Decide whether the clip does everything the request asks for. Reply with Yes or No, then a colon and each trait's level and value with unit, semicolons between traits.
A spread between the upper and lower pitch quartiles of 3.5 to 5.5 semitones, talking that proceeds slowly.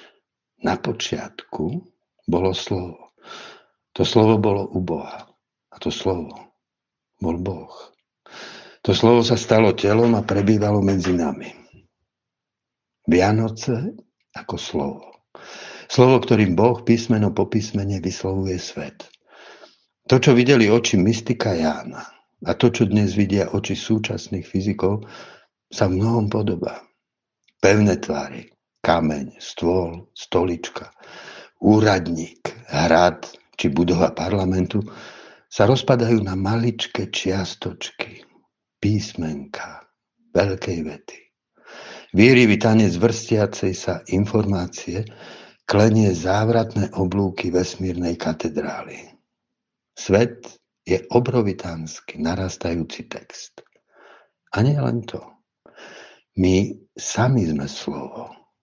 Yes: average, 3.8 semitones; slow, 95 wpm